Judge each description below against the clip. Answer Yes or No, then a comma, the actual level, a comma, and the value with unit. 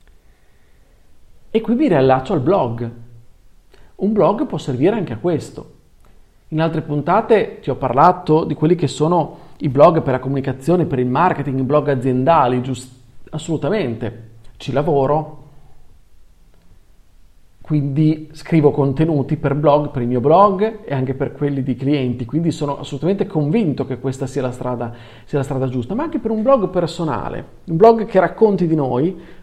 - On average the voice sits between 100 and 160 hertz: Yes, medium, 140 Hz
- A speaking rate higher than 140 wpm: Yes, average, 160 wpm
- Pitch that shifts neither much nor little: Yes, average, 4.6 semitones